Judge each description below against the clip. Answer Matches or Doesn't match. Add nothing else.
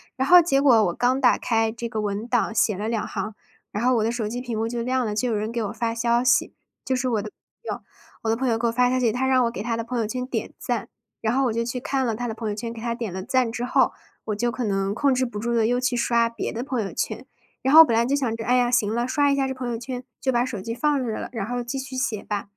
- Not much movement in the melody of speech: Matches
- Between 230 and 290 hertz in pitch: Matches